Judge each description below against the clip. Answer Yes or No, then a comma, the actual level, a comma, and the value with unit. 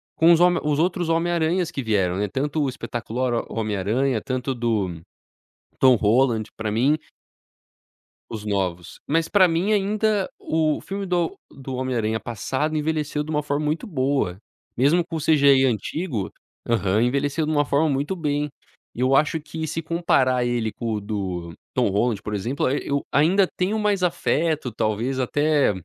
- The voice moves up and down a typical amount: No, wide, 5.7 semitones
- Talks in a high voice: No, medium, 140 Hz